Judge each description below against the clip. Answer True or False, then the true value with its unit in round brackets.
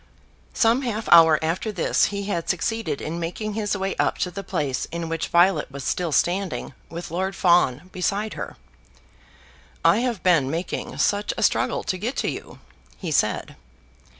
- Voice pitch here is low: False (180 Hz)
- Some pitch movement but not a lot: True (3.8 semitones)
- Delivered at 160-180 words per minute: True (170 wpm)